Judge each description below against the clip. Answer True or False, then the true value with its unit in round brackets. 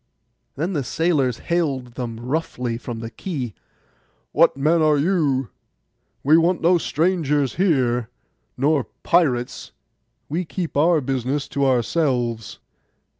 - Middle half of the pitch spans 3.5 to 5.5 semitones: True (4.9 semitones)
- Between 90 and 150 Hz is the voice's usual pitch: True (140 Hz)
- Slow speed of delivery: True (115 wpm)